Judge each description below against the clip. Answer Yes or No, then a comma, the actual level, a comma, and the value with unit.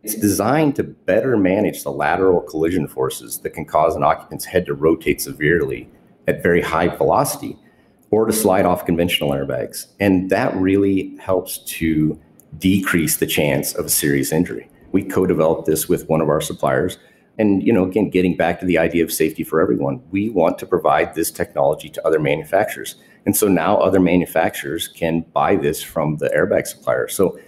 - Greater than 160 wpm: Yes, average, 180 wpm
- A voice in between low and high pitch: No, very low, 90 Hz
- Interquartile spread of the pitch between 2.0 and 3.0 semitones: No, average, 3.6 semitones